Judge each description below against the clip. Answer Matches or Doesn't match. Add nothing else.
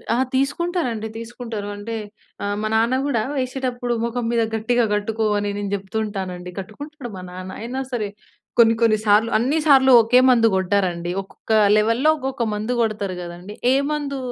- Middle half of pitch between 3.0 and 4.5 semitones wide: Matches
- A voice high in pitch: Matches